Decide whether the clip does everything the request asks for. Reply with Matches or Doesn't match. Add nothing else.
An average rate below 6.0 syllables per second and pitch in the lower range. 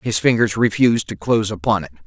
Doesn't match